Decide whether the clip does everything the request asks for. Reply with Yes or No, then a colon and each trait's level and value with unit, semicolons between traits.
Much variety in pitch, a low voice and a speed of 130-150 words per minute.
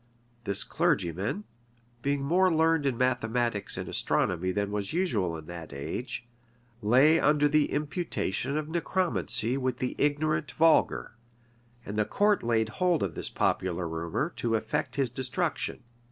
Yes: wide, 7.0 semitones; low, 125 Hz; average, 140 wpm